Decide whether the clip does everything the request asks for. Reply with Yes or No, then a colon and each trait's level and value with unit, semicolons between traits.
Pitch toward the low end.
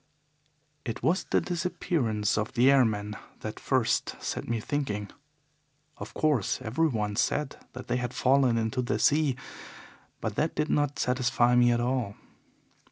Yes: low, 125 Hz